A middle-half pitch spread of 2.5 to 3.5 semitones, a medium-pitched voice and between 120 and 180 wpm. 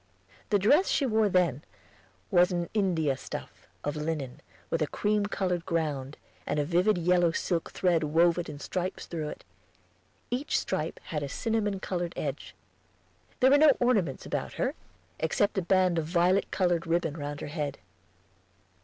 No: average, 4.2 semitones; medium, 175 Hz; average, 160 wpm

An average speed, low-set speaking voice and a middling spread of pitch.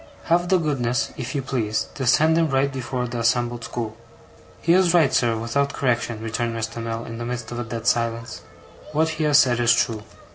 No: fast, 210 wpm; low, 120 Hz; average, 3.4 semitones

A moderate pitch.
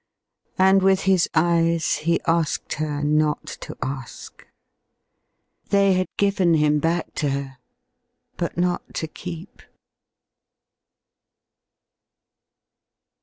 Yes: medium, 165 Hz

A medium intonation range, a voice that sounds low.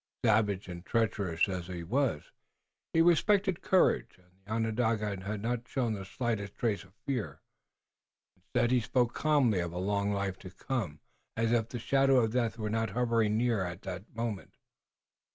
Yes: average, 3.7 semitones; low, 110 Hz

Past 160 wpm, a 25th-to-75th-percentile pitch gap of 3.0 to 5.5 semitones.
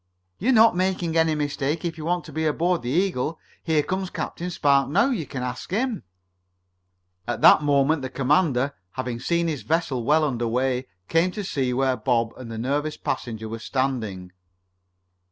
Yes: average, 170 wpm; average, 5.0 semitones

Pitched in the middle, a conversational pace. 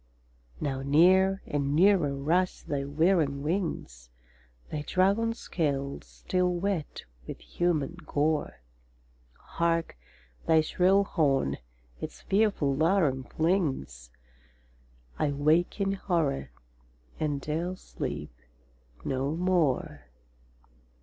No: medium, 155 Hz; slow, 95 wpm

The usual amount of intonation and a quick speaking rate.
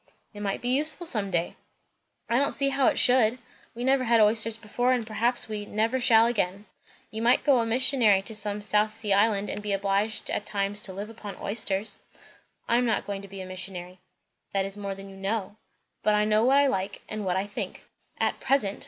Yes: average, 3.0 semitones; fast, 215 wpm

